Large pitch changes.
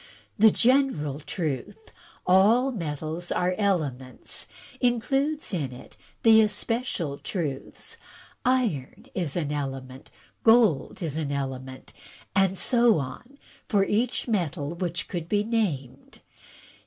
Yes: wide, 7.9 semitones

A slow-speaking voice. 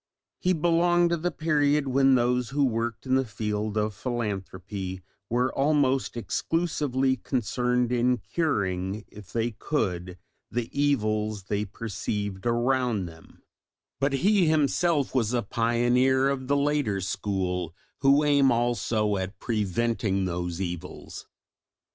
Yes: slow, 125 wpm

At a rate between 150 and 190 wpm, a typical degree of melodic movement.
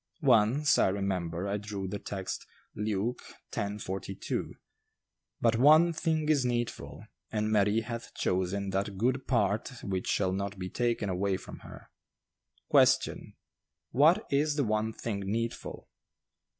No: slow, 135 wpm; average, 3.8 semitones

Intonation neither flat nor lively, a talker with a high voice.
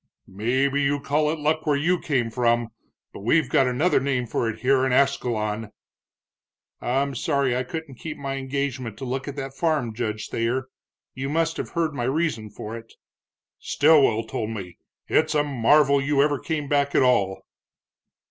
No: average, 3.6 semitones; low, 135 Hz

